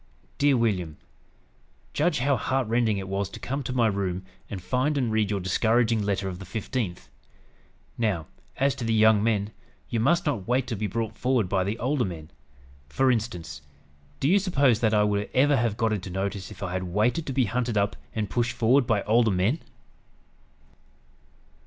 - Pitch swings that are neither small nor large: Yes, average, 4.2 semitones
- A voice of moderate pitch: No, low, 110 Hz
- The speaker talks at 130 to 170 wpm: No, average, 190 wpm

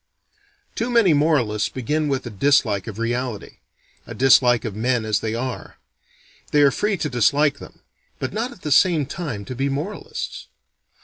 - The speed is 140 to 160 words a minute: No, average, 170 wpm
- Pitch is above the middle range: No, low, 135 Hz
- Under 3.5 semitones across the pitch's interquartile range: No, average, 4.8 semitones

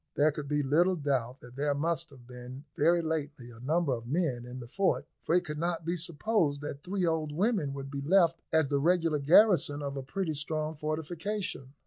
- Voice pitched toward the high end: No, medium, 150 Hz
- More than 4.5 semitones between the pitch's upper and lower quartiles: No, average, 3.5 semitones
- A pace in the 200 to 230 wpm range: Yes, fast, 205 wpm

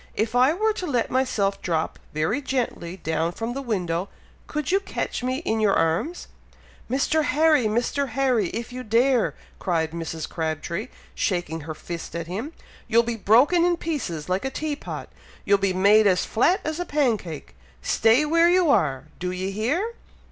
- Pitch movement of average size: No, wide, 7.9 semitones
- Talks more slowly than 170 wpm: No, average, 175 wpm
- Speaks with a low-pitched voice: No, high, 225 Hz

